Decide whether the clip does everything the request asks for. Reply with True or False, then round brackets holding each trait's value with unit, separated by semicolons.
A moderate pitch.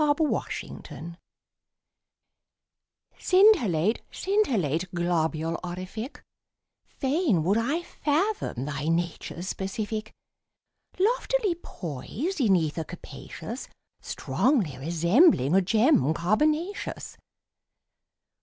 False (205 Hz)